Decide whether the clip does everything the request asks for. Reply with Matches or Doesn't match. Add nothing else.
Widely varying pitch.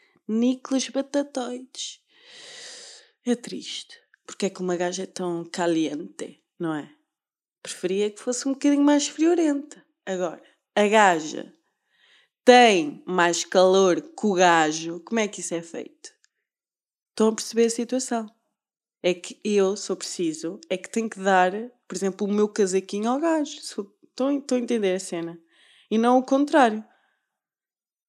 Matches